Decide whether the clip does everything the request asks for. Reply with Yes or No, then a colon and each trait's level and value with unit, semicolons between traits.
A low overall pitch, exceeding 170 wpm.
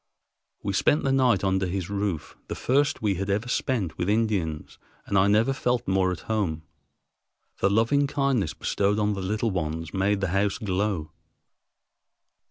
No: low, 100 Hz; average, 165 wpm